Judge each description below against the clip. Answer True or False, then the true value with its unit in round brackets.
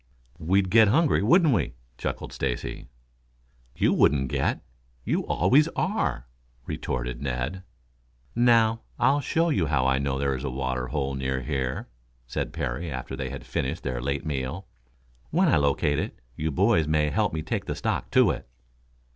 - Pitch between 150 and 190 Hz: False (75 Hz)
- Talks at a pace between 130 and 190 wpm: True (165 wpm)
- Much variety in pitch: True (7.3 semitones)